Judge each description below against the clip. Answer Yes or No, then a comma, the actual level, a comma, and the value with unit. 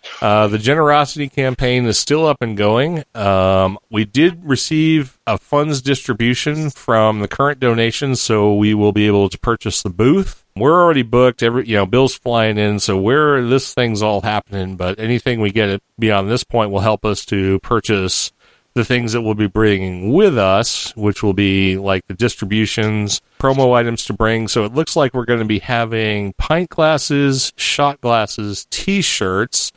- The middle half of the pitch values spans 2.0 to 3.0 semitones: No, average, 4.2 semitones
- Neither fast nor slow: Yes, average, 175 wpm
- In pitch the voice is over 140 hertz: No, low, 115 Hz